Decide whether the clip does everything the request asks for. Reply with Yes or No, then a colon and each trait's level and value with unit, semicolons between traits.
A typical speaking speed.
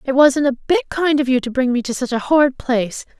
No: fast, 280 wpm